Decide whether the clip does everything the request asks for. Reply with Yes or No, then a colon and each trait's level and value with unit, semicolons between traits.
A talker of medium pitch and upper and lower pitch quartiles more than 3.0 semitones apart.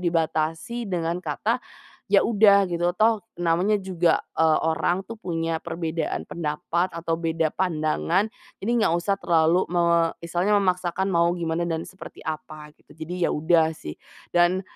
No: medium, 170 Hz; narrow, 2.4 semitones